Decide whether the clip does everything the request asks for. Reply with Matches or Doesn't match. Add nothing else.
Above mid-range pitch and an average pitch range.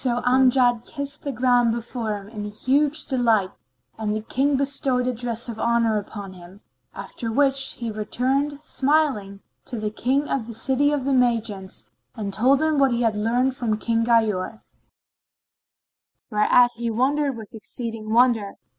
Matches